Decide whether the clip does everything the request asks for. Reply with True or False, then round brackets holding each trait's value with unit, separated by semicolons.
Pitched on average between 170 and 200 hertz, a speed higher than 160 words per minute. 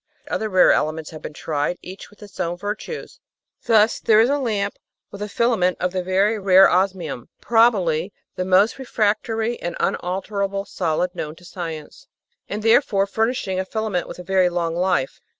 True (190 Hz; 170 wpm)